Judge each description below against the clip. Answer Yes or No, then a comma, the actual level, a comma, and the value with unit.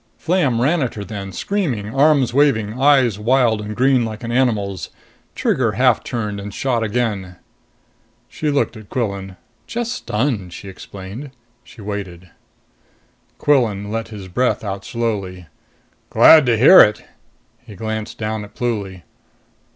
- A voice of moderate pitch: No, low, 110 Hz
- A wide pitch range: No, average, 4.2 semitones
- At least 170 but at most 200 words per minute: No, average, 140 wpm